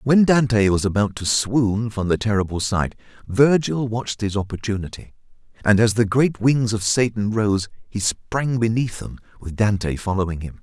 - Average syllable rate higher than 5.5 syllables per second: No, 4.8 syllables/s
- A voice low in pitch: Yes, low, 110 Hz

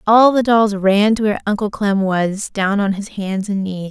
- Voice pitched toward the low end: No, high, 205 Hz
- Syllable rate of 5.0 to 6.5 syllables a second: No, 4.6 syllables/s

